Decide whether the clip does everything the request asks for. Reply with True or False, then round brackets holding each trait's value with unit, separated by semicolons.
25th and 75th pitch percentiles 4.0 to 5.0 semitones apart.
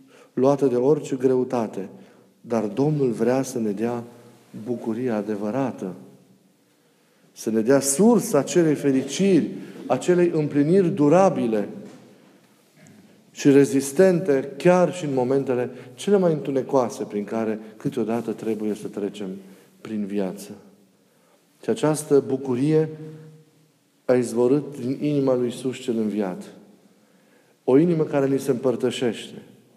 True (4.4 semitones)